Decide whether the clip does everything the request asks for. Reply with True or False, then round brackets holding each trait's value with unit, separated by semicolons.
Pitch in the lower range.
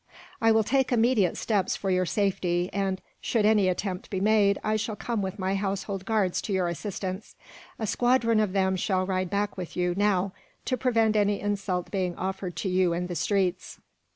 False (195 Hz)